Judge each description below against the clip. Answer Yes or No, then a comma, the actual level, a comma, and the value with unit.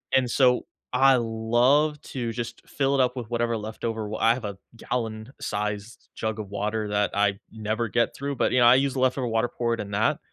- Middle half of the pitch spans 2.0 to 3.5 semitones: Yes, narrow, 2.6 semitones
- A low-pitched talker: Yes, low, 115 Hz